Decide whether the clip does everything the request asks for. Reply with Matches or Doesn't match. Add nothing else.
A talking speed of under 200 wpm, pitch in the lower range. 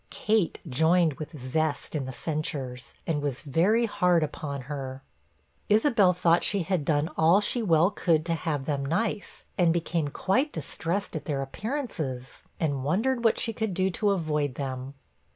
Doesn't match